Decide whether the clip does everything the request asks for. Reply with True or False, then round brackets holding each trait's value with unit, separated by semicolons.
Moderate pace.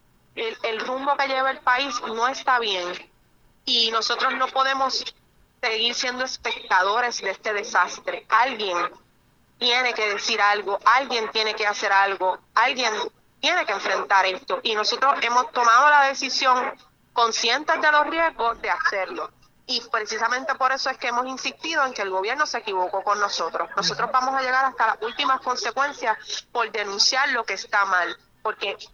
True (160 wpm)